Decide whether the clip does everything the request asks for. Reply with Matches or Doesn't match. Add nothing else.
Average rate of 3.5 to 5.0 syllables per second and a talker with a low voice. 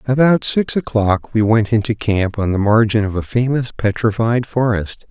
Matches